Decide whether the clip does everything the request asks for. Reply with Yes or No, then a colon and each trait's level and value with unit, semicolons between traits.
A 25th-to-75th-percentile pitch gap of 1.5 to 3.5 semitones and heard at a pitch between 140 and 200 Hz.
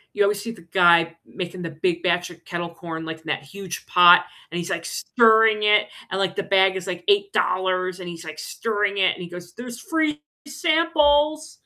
No: average, 4.5 semitones; medium, 185 Hz